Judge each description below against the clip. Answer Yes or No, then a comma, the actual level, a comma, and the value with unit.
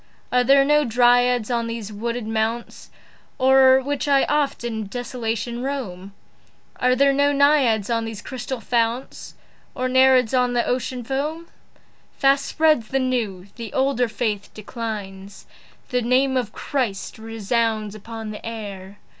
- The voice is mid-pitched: No, high, 240 Hz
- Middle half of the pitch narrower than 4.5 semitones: Yes, average, 3.1 semitones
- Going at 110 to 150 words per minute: Yes, average, 140 wpm